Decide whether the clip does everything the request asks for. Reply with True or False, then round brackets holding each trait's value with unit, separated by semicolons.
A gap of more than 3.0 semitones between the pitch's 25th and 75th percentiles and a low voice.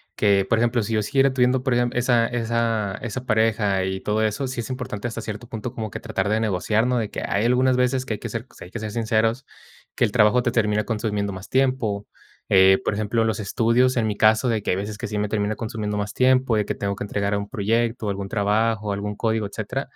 False (2.5 semitones; 110 Hz)